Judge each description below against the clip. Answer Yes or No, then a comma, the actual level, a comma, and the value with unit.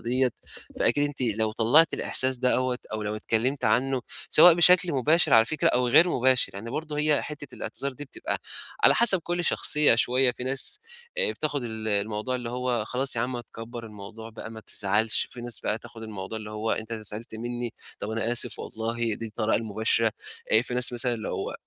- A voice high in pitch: No, low, 120 Hz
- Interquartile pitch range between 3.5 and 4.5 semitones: No, average, 3.1 semitones